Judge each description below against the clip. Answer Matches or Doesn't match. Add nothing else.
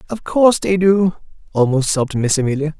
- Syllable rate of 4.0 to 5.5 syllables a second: Doesn't match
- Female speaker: Doesn't match